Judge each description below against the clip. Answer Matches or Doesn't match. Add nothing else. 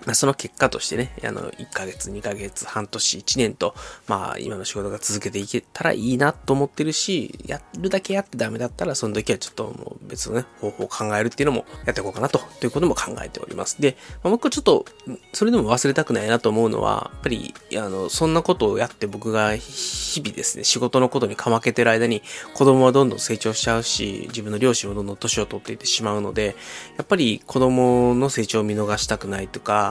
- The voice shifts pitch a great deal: Doesn't match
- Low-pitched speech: Matches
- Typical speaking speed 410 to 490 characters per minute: Matches